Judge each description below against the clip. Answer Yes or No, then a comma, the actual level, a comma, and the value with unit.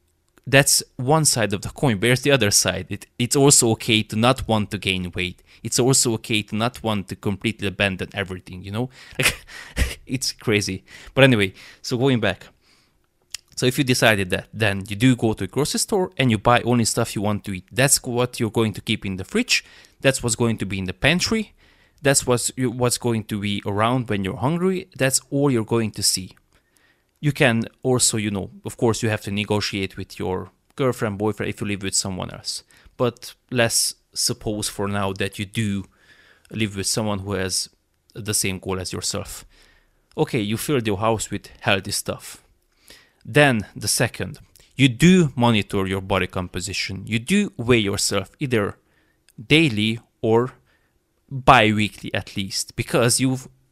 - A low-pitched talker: Yes, low, 110 Hz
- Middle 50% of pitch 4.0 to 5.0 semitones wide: Yes, average, 4.3 semitones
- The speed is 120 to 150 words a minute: No, average, 180 wpm